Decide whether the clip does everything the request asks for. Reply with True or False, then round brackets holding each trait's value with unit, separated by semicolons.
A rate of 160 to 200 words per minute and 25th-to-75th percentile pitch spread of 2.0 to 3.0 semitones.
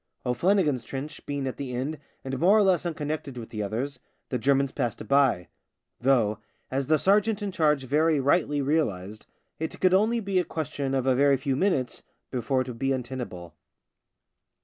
False (180 wpm; 3.9 semitones)